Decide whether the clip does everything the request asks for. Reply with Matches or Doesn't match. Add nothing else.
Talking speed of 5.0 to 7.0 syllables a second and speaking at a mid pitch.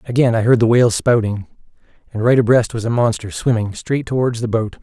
Doesn't match